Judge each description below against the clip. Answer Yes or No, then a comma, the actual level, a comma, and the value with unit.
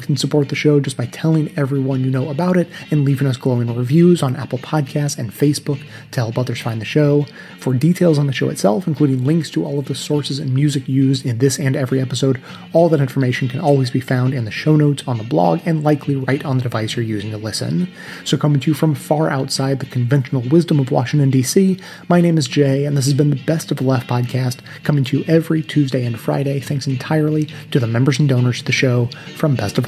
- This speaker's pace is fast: Yes, fast, 240 wpm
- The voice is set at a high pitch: No, medium, 140 Hz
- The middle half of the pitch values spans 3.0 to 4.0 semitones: No, narrow, 2.6 semitones